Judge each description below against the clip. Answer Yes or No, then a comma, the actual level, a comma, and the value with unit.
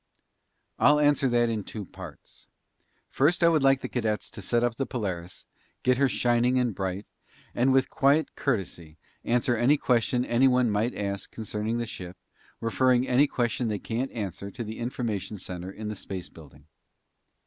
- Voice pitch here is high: No, low, 120 Hz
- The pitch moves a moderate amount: Yes, average, 3.9 semitones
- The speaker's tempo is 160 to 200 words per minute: Yes, average, 170 wpm